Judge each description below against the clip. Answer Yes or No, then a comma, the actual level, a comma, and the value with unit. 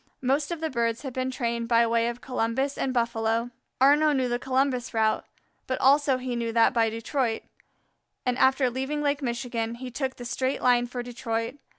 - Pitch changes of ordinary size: No, narrow, 2.3 semitones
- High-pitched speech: Yes, very high, 250 Hz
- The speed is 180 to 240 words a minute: Yes, average, 190 wpm